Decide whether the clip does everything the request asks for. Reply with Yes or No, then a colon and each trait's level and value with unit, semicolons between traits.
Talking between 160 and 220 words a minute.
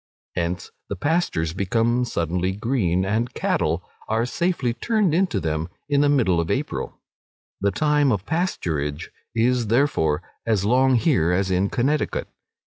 No: average, 140 wpm